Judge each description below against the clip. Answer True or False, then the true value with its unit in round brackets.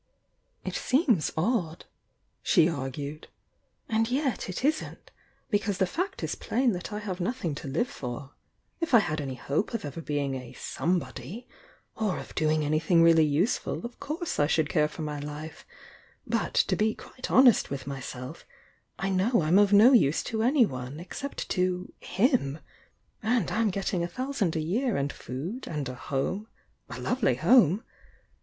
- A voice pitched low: False (180 Hz)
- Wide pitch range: True (7.6 semitones)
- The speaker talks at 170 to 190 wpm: True (175 wpm)